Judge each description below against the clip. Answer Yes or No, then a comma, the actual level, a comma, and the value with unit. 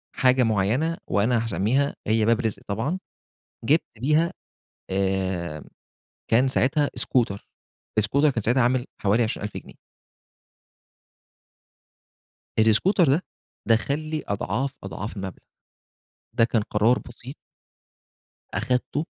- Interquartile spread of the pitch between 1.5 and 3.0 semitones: No, average, 4.6 semitones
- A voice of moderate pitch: No, low, 115 Hz